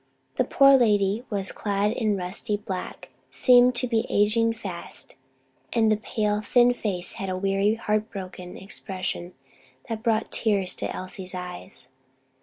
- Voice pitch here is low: No, high, 205 Hz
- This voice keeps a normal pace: Yes, average, 150 wpm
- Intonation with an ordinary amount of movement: Yes, average, 3.1 semitones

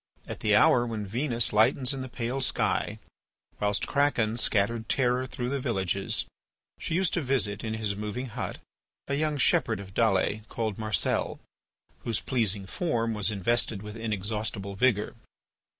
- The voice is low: Yes, low, 115 Hz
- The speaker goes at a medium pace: Yes, average, 150 wpm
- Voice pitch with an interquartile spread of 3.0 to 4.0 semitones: Yes, average, 3.5 semitones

